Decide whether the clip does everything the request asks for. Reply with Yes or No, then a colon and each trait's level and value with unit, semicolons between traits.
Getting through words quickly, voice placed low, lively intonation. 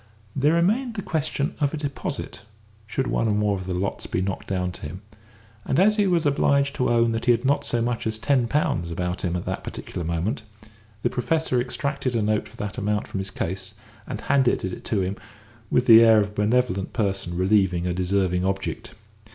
Yes: fast, 210 wpm; low, 110 Hz; wide, 6.4 semitones